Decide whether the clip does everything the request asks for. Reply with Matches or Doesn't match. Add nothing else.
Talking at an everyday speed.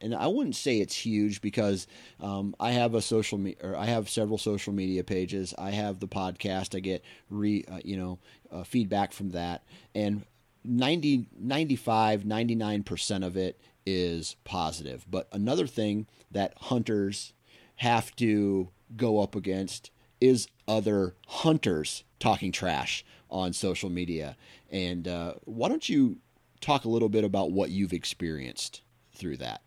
Matches